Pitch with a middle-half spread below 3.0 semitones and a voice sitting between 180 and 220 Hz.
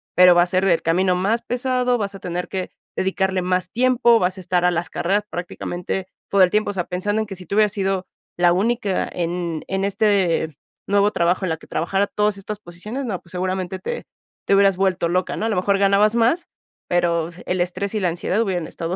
Yes: narrow, 2.6 semitones; high, 190 Hz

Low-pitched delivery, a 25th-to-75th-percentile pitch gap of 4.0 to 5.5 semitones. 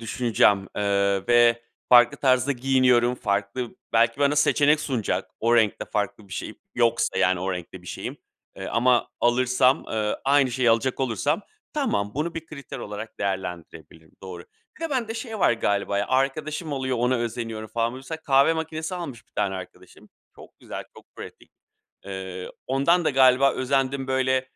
Yes: low, 125 Hz; average, 4.8 semitones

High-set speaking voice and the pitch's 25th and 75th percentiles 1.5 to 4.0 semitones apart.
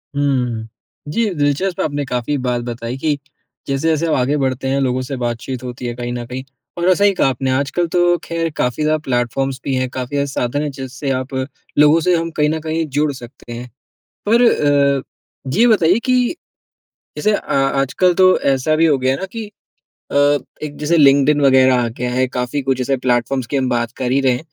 No: low, 135 Hz; average, 3.6 semitones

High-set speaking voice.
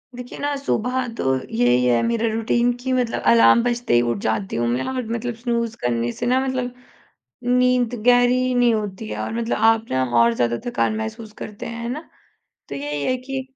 Yes: high, 230 Hz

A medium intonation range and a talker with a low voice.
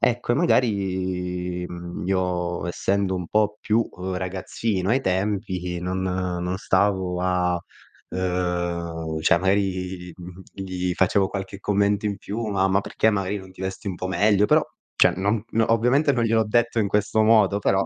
No: narrow, 2.3 semitones; very low, 95 Hz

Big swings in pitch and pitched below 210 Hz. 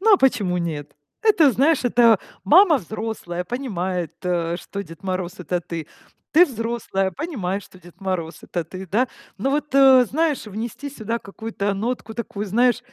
No: wide, 6.1 semitones; high, 215 Hz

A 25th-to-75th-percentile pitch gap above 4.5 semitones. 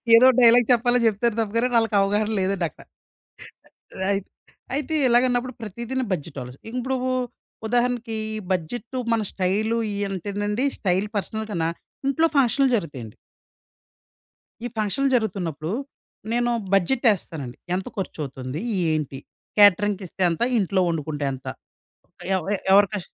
Yes: average, 5.0 semitones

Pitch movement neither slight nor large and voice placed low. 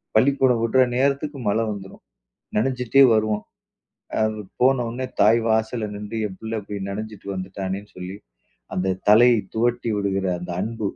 Yes: average, 3.2 semitones; low, 110 Hz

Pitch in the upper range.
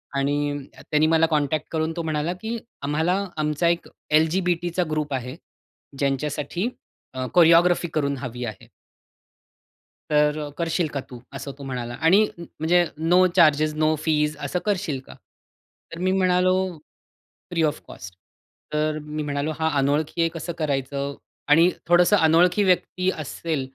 No: medium, 155 Hz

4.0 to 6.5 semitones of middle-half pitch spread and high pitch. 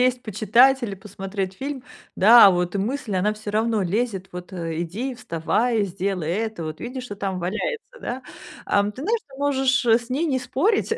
Yes: average, 5.2 semitones; high, 220 Hz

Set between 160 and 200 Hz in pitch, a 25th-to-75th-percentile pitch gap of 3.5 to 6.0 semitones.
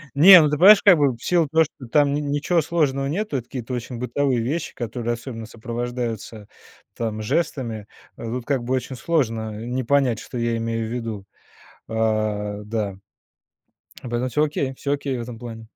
No: low, 120 Hz; average, 3.9 semitones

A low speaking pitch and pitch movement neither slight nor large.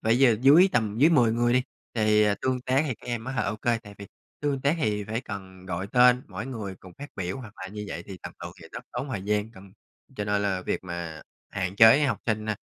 Yes: low, 110 Hz; average, 4.1 semitones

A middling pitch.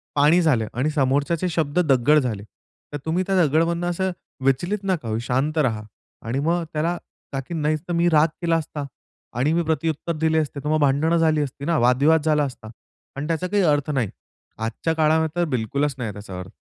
Yes: medium, 150 Hz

